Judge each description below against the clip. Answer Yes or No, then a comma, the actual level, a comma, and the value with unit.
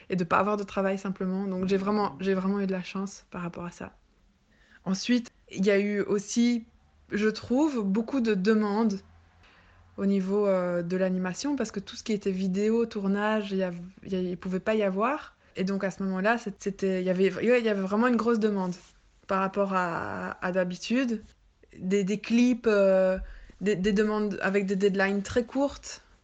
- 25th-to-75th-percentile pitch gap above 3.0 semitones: No, narrow, 2.4 semitones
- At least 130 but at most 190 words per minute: Yes, average, 185 wpm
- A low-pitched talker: No, high, 200 Hz